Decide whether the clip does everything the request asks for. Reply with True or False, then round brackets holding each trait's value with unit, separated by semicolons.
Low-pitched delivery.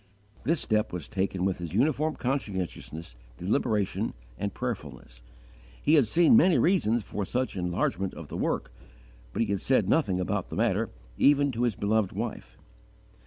True (105 Hz)